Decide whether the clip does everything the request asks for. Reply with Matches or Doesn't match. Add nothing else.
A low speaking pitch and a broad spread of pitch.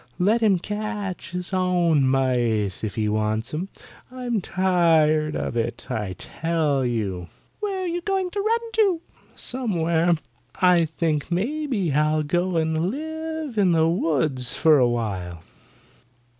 Doesn't match